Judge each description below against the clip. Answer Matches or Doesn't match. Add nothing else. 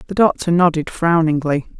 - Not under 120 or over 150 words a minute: Matches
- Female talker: Matches